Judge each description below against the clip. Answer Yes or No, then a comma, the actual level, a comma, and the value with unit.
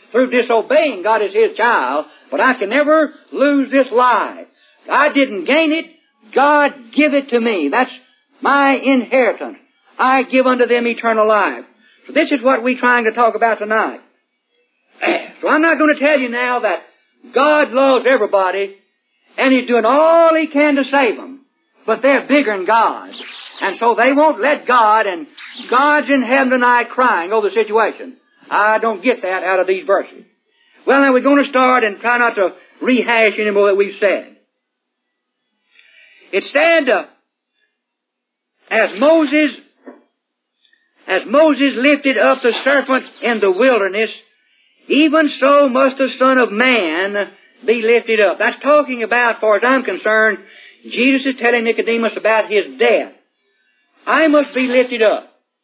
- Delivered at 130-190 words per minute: Yes, average, 160 wpm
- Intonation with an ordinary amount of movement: Yes, average, 4.3 semitones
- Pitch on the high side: Yes, very high, 255 Hz